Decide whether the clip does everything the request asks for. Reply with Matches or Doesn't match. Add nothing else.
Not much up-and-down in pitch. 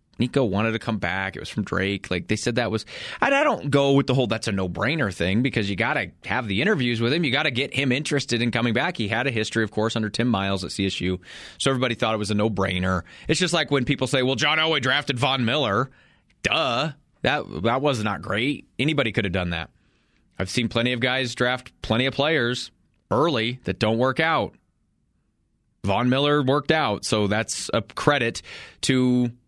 Doesn't match